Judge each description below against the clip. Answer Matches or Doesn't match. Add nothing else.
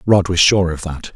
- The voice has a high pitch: Doesn't match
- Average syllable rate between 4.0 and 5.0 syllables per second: Matches